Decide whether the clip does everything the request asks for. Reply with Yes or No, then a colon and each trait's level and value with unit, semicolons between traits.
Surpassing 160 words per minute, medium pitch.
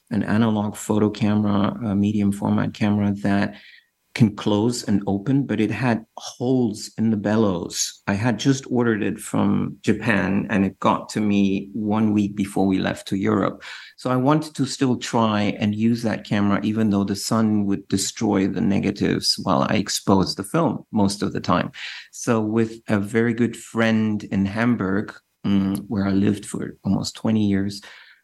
No: average, 170 wpm; low, 105 Hz